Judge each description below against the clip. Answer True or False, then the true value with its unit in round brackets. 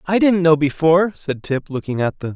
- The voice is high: False (160 Hz)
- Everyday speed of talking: False (230 wpm)